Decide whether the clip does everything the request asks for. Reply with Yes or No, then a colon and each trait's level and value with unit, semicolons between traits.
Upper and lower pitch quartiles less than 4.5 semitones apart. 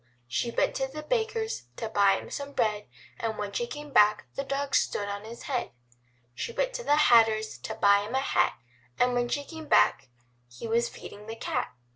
No: average, 5.3 semitones